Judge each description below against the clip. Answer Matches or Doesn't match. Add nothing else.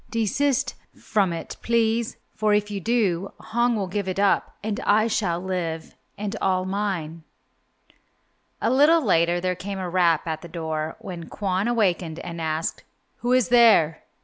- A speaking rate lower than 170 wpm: Matches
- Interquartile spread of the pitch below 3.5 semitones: Doesn't match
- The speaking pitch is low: Doesn't match